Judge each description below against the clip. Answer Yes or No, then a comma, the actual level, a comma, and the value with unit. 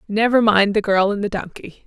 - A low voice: No, high, 210 Hz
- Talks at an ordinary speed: No, fast, 225 wpm